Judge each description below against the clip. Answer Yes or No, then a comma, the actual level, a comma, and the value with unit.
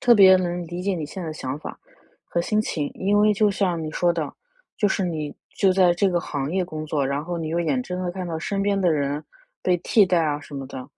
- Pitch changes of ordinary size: Yes, average, 3.6 semitones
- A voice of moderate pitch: Yes, medium, 175 Hz